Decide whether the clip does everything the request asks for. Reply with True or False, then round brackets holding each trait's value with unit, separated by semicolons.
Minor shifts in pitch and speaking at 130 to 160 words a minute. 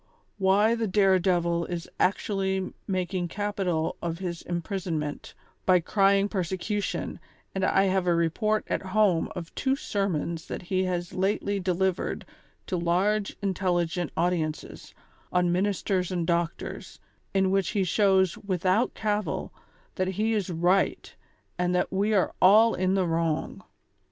True (2.2 semitones; 145 wpm)